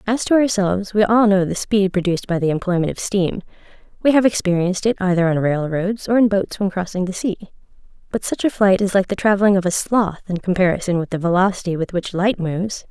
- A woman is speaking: Yes, female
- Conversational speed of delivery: No, fast, 225 wpm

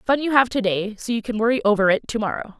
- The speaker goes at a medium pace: No, fast, 300 wpm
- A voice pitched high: Yes, high, 230 Hz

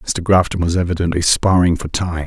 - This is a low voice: Yes, very low, 85 Hz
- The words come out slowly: No, average, 185 wpm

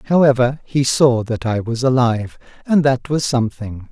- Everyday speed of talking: Yes, average, 170 wpm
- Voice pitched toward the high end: No, low, 125 Hz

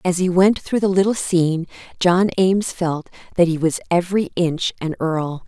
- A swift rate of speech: No, average, 185 wpm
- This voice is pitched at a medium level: Yes, medium, 175 Hz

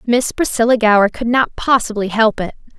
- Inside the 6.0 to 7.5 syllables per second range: No, 5.3 syllables/s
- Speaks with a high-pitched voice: Yes, high, 225 Hz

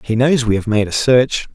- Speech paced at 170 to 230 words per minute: No, fast, 270 wpm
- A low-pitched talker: Yes, low, 120 Hz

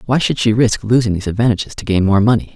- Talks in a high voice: No, low, 105 Hz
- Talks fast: Yes, fast, 260 wpm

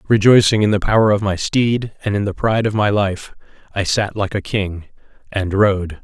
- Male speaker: Yes, male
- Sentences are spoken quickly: Yes, fast, 210 wpm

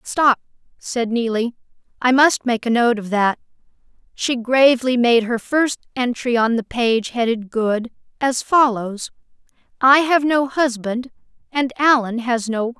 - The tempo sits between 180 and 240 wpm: No, average, 150 wpm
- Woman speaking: Yes, female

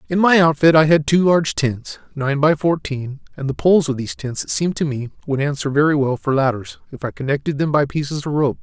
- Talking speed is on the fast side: Yes, fast, 245 wpm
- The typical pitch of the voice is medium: Yes, medium, 145 Hz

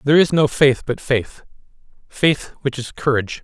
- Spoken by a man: Yes, male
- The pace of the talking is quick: No, average, 155 wpm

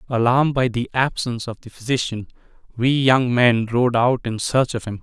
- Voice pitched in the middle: No, low, 120 Hz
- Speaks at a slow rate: No, average, 190 wpm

